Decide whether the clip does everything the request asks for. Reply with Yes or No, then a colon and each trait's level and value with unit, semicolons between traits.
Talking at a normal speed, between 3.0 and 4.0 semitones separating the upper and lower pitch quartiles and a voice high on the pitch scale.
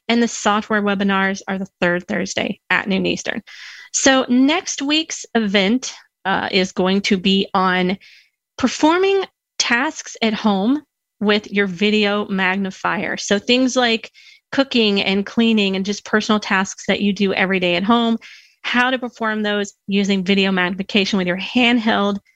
Yes: average, 150 wpm; average, 3.6 semitones; high, 205 Hz